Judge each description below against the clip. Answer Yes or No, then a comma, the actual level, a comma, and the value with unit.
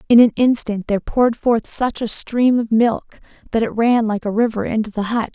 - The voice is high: Yes, high, 225 Hz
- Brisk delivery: Yes, fast, 225 wpm